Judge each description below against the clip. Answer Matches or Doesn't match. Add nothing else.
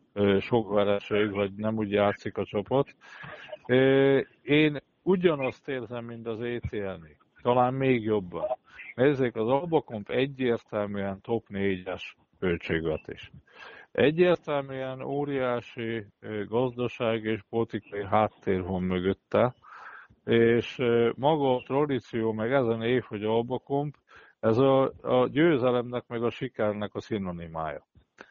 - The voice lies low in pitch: Matches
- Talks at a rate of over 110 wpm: Doesn't match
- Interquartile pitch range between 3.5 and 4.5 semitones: Matches